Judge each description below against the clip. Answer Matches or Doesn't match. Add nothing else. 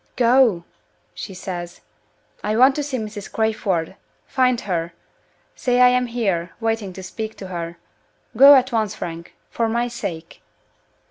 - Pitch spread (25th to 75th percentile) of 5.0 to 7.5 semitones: Matches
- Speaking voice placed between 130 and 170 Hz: Doesn't match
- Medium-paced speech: Matches